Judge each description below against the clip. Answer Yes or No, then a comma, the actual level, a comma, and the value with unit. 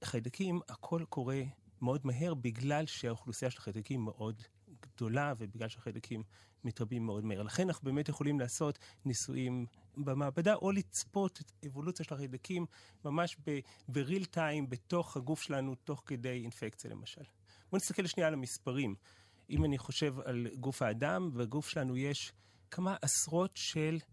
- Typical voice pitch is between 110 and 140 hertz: Yes, low, 135 Hz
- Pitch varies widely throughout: No, average, 4.7 semitones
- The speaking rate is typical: Yes, average, 140 wpm